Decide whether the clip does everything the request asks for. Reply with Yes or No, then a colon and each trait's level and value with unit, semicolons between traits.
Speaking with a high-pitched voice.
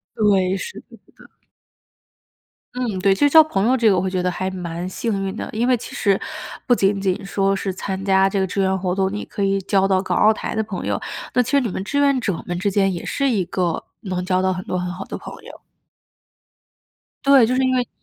Yes: high, 195 Hz